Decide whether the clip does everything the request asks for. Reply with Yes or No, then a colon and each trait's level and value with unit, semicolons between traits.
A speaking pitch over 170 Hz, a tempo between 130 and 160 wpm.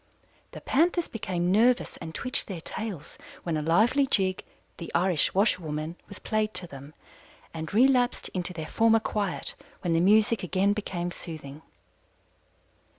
Yes: medium, 185 Hz; average, 145 wpm